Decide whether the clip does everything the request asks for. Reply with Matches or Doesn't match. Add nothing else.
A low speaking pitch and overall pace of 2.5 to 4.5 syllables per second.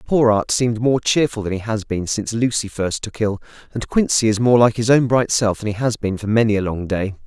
Doesn't match